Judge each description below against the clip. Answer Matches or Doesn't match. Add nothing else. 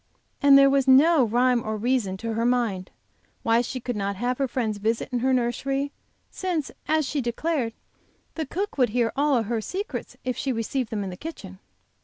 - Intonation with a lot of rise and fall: Doesn't match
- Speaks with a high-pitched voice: Matches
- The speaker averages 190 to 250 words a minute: Matches